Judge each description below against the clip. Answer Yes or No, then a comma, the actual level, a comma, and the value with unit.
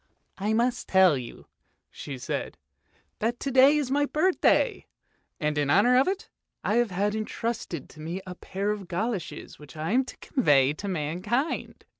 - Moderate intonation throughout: No, wide, 7.2 semitones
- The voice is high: Yes, high, 205 Hz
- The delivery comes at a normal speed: Yes, average, 180 wpm